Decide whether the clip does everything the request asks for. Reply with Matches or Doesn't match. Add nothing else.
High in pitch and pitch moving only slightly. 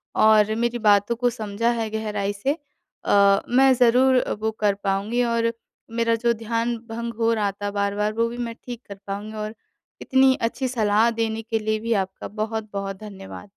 Matches